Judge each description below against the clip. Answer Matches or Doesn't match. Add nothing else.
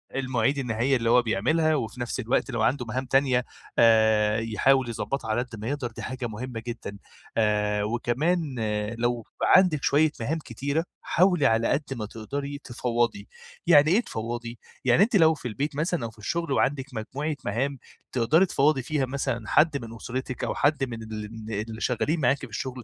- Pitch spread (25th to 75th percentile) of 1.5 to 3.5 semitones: Doesn't match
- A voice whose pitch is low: Matches